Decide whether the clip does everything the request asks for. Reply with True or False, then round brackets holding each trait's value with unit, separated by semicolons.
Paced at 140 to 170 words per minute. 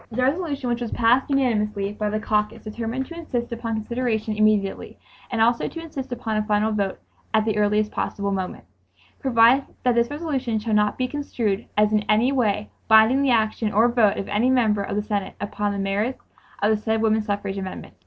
False (200 wpm)